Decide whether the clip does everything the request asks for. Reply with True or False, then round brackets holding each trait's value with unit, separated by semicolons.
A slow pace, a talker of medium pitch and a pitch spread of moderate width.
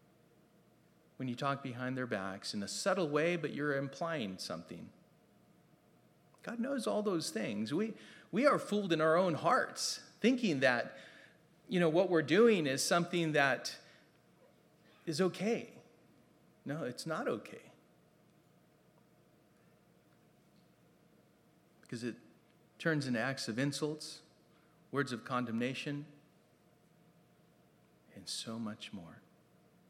True (115 wpm; 155 Hz; 4.8 semitones)